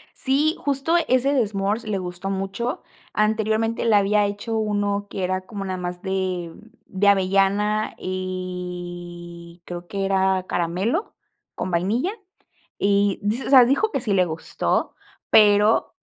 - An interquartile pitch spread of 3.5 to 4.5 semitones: No, average, 2.9 semitones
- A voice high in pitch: Yes, high, 200 Hz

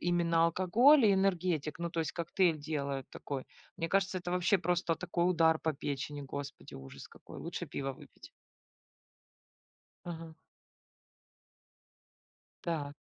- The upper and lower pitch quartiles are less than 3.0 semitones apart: No, average, 3.4 semitones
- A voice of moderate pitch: Yes, medium, 165 Hz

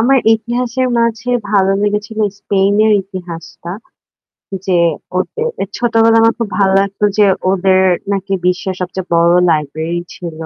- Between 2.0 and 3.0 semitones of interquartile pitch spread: No, average, 3.7 semitones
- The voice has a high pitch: Yes, high, 195 Hz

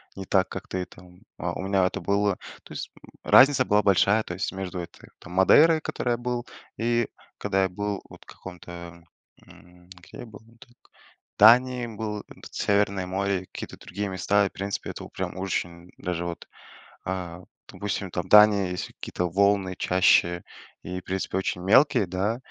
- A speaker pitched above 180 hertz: No, very low, 95 Hz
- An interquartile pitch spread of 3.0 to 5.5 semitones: No, narrow, 2.6 semitones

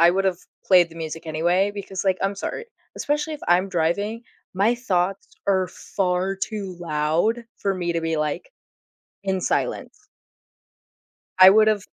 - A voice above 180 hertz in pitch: Yes, high, 190 Hz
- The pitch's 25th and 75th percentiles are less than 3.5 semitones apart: Yes, average, 2.8 semitones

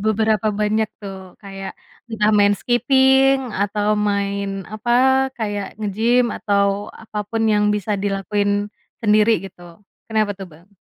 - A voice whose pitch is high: Yes, high, 210 Hz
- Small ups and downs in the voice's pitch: Yes, narrow, 1.8 semitones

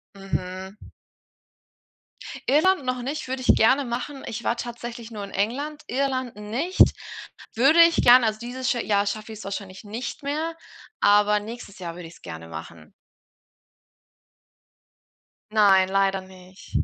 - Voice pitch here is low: No, high, 220 Hz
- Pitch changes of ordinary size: Yes, average, 4.7 semitones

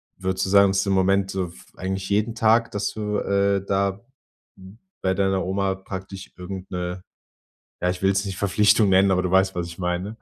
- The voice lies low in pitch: Yes, very low, 95 Hz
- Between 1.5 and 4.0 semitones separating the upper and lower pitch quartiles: No, narrow, 1.0 semitones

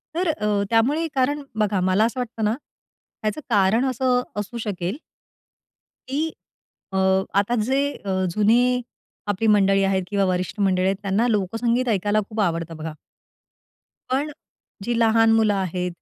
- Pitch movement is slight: No, average, 4.0 semitones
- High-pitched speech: Yes, high, 210 Hz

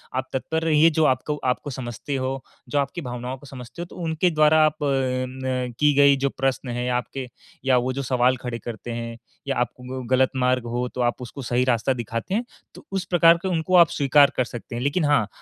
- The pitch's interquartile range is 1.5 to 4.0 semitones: Yes, average, 3.0 semitones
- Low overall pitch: Yes, low, 130 Hz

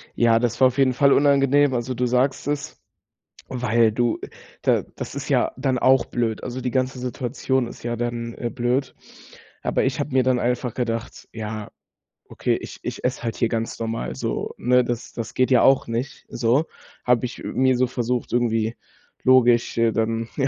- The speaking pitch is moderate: No, low, 125 Hz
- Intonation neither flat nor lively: No, narrow, 2.0 semitones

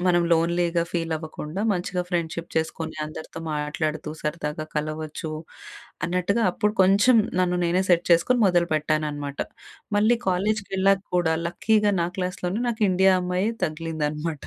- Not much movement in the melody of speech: No, average, 3.2 semitones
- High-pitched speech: No, medium, 170 Hz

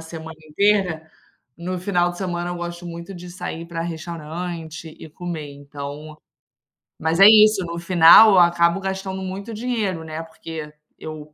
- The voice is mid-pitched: Yes, medium, 170 Hz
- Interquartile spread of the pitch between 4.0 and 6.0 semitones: No, narrow, 2.5 semitones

